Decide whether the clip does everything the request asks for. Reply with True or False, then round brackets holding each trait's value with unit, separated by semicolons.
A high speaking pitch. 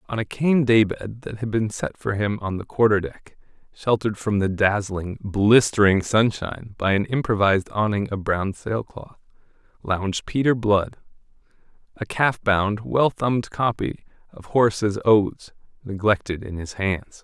False (105 Hz)